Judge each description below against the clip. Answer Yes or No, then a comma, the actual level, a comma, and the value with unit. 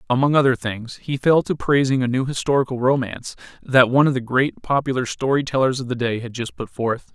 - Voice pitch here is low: Yes, low, 130 Hz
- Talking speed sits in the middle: No, fast, 220 wpm